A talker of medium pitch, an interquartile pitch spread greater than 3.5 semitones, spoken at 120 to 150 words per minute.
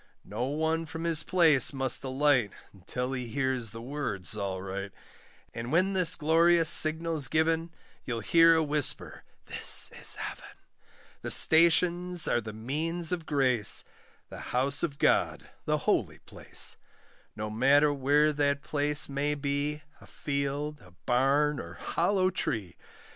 Yes: medium, 145 Hz; average, 4.1 semitones; average, 140 wpm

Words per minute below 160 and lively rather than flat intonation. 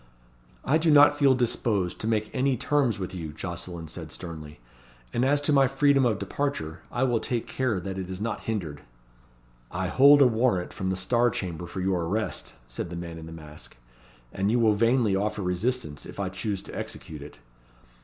No: average, 195 wpm; wide, 6.2 semitones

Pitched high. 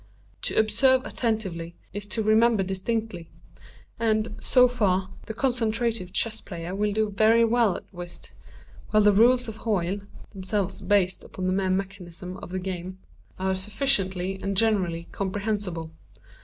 Yes: high, 200 Hz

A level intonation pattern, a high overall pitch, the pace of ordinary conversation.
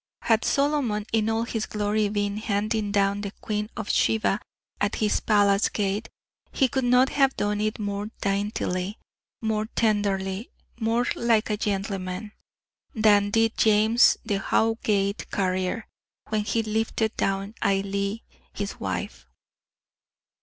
No: narrow, 1.9 semitones; high, 210 Hz; slow, 130 wpm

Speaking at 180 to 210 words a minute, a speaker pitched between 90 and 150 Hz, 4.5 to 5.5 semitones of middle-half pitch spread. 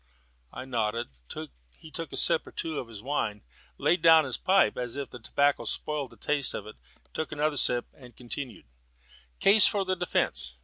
Yes: average, 185 wpm; medium, 140 Hz; average, 4.8 semitones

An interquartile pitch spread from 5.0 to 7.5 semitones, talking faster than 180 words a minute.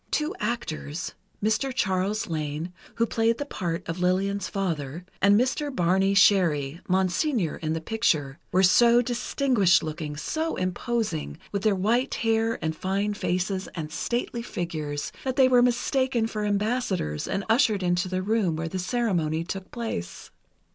No: wide, 5.6 semitones; average, 140 wpm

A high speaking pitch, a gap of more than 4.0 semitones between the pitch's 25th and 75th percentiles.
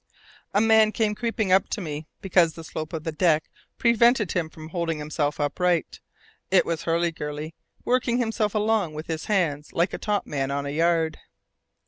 No: medium, 170 Hz; average, 5.2 semitones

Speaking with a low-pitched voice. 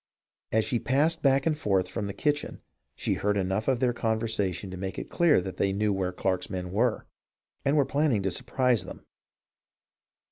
Yes: low, 110 Hz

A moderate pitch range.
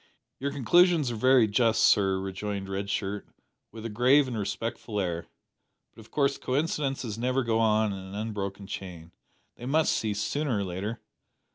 Yes: average, 4.4 semitones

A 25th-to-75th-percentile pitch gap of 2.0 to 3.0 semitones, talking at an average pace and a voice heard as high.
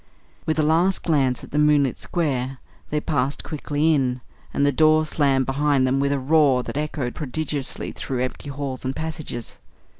No: average, 2.7 semitones; average, 175 wpm; medium, 145 Hz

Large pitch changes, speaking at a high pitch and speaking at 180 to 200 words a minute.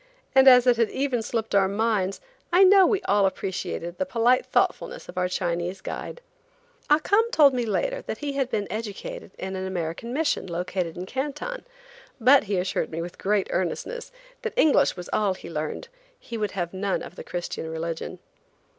Yes: wide, 7.0 semitones; high, 210 Hz; average, 185 wpm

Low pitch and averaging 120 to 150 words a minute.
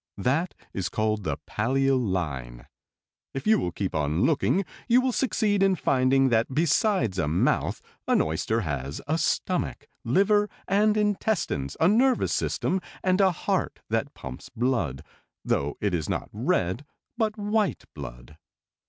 Yes: low, 130 Hz; average, 145 wpm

